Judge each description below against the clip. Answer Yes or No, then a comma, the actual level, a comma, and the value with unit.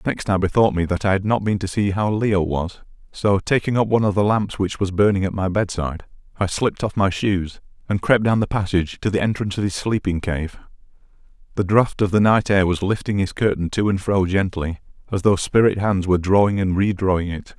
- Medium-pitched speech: No, low, 100 Hz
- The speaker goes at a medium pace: No, fast, 230 wpm